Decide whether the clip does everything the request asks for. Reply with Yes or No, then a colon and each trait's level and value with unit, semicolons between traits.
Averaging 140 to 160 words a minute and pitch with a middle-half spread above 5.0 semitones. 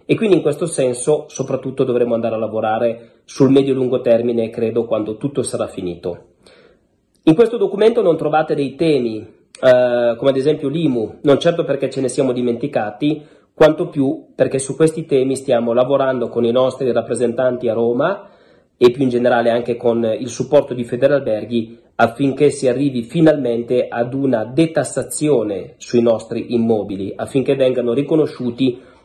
No: average, 155 wpm; average, 3.2 semitones